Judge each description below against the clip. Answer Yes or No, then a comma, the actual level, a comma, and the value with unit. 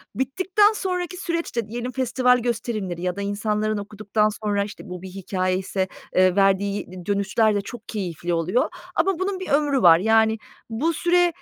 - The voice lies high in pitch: Yes, high, 215 Hz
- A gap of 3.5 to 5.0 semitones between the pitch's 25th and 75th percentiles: No, wide, 5.5 semitones